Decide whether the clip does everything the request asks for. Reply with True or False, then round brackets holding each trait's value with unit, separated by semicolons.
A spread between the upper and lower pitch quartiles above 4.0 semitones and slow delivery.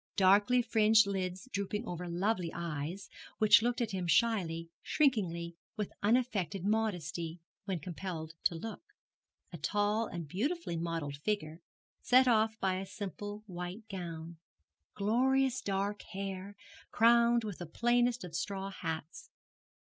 True (4.5 semitones; 130 wpm)